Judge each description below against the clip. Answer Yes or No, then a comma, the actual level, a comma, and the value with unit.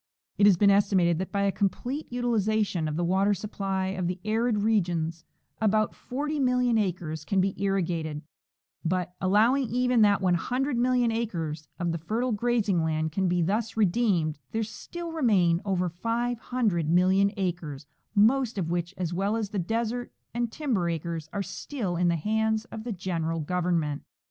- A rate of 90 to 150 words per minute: No, average, 160 wpm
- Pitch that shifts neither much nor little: Yes, average, 4.7 semitones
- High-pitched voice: Yes, high, 195 Hz